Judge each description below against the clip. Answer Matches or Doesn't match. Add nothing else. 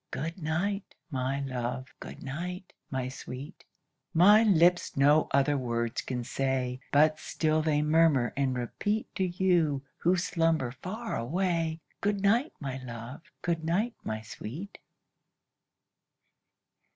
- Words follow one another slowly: Matches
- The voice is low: Doesn't match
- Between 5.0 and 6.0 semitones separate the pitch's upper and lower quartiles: Matches